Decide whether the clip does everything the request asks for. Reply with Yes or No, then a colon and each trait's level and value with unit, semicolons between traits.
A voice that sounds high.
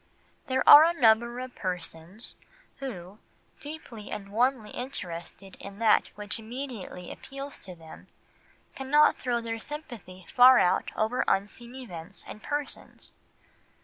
Yes: high, 230 Hz